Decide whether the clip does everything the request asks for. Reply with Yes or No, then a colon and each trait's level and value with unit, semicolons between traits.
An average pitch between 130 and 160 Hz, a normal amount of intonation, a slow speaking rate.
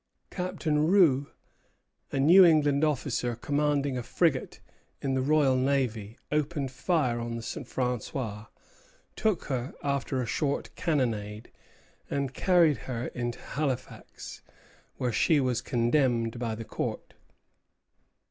Yes: low, 135 Hz; average, 3.8 semitones; slow, 120 wpm